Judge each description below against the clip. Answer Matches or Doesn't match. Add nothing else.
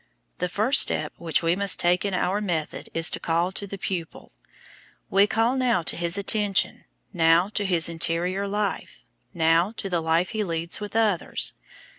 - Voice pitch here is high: Doesn't match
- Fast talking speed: Doesn't match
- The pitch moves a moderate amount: Matches